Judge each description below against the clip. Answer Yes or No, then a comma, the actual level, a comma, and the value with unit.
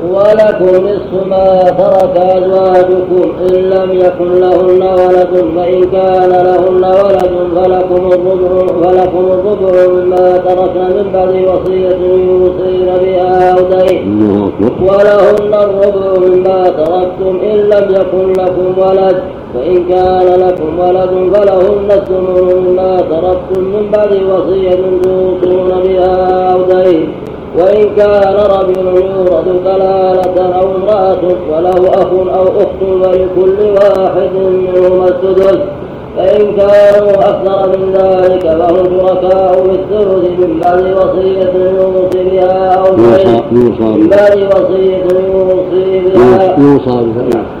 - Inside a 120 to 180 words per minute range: No, average, 105 wpm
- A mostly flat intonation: Yes, narrow, 0.7 semitones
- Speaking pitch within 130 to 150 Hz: No, medium, 185 Hz